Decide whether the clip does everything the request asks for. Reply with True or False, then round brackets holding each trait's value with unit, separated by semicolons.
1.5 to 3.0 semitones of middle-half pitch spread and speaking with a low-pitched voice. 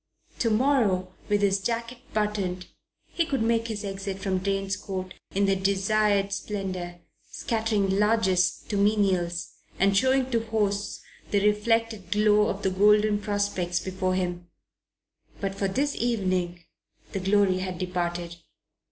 False (2.4 semitones; 200 Hz)